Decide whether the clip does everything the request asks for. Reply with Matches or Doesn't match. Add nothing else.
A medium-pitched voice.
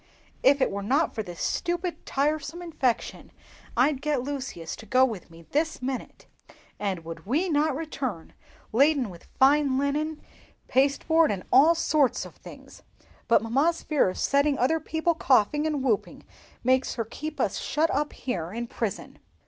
Doesn't match